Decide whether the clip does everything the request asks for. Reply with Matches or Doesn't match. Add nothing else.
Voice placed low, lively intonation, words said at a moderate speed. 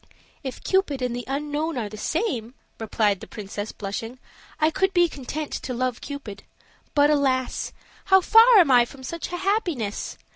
Doesn't match